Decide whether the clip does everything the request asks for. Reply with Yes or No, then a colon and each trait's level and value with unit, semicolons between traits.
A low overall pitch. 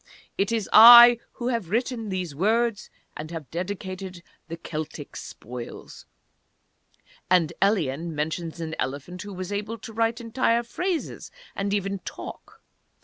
No: high, 195 Hz